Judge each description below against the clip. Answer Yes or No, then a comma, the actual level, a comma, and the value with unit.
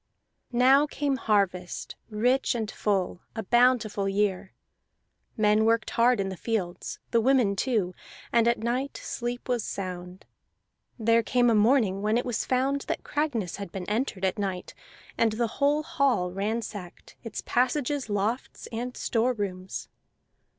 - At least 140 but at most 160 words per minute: Yes, average, 145 wpm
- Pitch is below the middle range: No, high, 225 Hz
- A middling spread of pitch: Yes, average, 3.9 semitones